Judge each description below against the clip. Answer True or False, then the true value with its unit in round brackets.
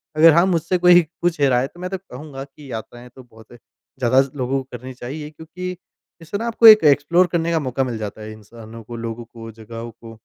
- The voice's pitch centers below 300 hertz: True (135 Hz)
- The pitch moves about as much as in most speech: False (6.3 semitones)